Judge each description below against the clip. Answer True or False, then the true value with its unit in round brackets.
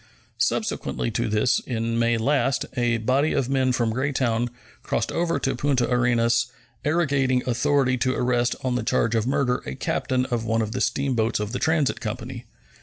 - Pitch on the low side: True (125 Hz)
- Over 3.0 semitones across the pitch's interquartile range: False (2.5 semitones)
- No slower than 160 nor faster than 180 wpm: True (175 wpm)